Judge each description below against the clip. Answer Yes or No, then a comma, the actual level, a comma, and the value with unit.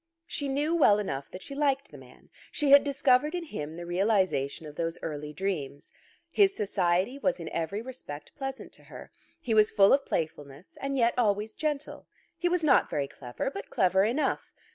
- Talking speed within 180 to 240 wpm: Yes, average, 185 wpm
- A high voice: Yes, high, 210 Hz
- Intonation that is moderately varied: No, wide, 8.8 semitones